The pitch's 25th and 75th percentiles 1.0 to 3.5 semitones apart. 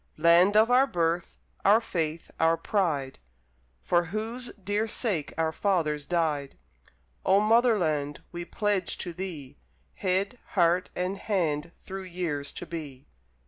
No: average, 4.2 semitones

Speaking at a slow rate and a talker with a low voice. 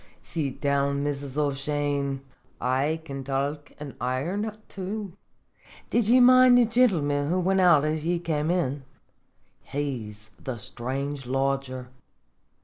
No: slow, 125 wpm; medium, 145 Hz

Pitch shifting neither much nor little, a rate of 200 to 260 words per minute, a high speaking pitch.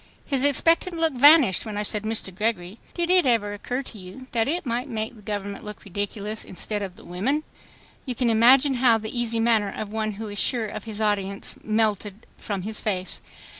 Yes: average, 3.3 semitones; fast, 205 wpm; high, 220 Hz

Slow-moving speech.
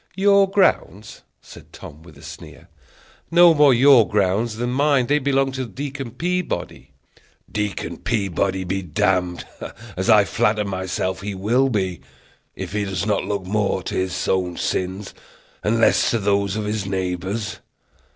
No: average, 160 wpm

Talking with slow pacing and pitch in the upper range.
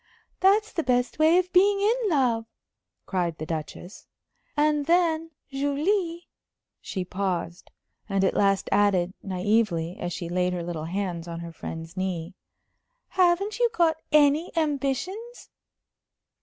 Yes: slow, 130 wpm; high, 245 Hz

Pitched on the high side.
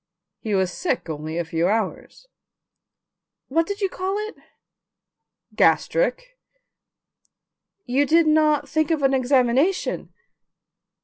Yes: very high, 285 Hz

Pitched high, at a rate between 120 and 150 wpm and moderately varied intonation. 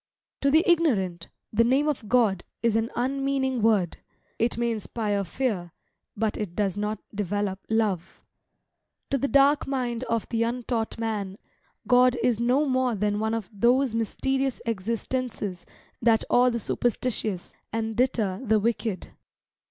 Yes: high, 230 Hz; average, 145 wpm; average, 3.4 semitones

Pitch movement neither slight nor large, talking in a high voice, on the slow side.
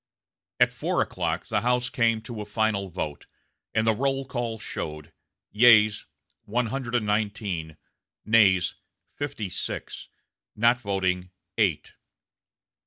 No: average, 3.5 semitones; low, 110 Hz; slow, 120 wpm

